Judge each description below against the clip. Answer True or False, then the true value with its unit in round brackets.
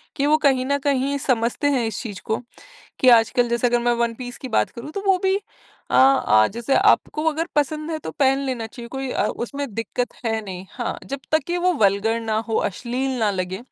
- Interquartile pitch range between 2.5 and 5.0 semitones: True (3.7 semitones)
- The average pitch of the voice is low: False (250 Hz)